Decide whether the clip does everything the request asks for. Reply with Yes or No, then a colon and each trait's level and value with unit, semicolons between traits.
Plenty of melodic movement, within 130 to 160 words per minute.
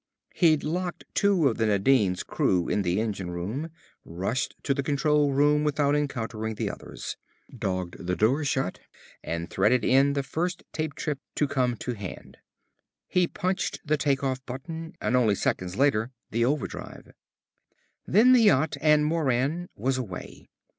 Yes: wide, 5.8 semitones; average, 155 wpm